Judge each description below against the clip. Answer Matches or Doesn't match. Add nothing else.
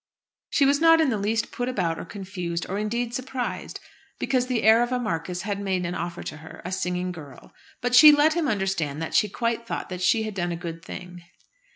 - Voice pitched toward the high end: Matches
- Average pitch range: Doesn't match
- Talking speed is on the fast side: Matches